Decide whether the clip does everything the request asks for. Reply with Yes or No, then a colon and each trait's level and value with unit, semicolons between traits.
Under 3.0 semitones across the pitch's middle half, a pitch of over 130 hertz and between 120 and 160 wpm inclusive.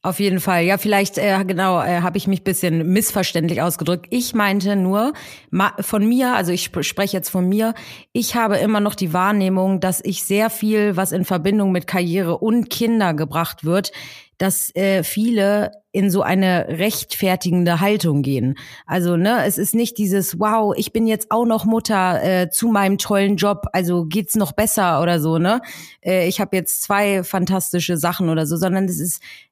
No: narrow, 2.6 semitones; high, 190 Hz; fast, 190 wpm